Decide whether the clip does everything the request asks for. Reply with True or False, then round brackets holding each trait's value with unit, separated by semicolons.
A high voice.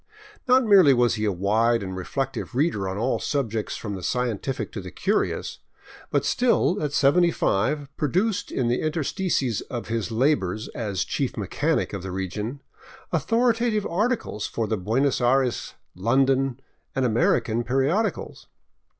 False (125 Hz)